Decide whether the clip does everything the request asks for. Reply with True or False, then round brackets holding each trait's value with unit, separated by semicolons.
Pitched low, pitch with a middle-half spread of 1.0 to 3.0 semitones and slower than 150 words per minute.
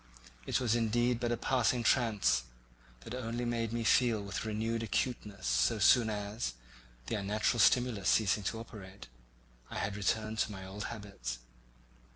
False (110 Hz; 2.7 semitones; 155 wpm)